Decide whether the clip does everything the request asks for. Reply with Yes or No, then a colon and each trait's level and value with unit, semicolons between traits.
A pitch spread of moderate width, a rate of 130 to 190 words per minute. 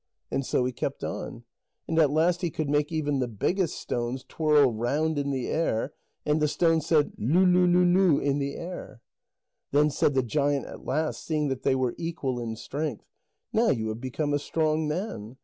No: average, 3.6 semitones; average, 200 wpm